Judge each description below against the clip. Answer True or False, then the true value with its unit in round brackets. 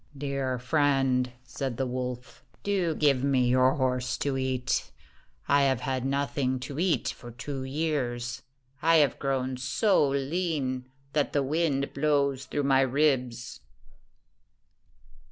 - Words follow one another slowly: True (130 wpm)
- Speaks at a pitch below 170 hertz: True (135 Hz)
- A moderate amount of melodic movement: False (2.1 semitones)